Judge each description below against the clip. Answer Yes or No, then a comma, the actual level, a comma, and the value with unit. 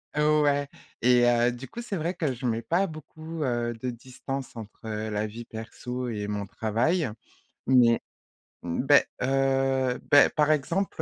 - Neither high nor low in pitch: No, low, 130 Hz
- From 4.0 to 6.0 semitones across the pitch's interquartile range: Yes, average, 4.3 semitones